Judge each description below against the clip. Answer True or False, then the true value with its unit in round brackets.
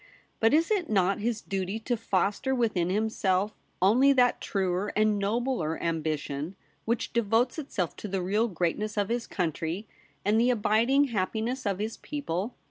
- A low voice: False (210 Hz)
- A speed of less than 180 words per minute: True (155 wpm)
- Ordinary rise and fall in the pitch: True (4.1 semitones)